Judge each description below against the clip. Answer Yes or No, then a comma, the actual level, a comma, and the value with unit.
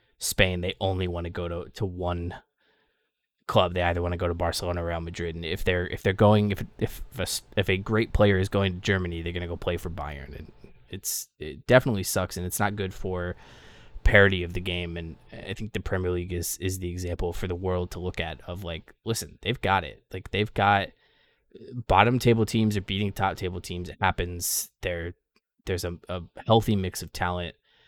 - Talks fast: Yes, fast, 215 wpm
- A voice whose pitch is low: Yes, very low, 90 Hz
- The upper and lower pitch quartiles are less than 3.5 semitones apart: Yes, narrow, 2.6 semitones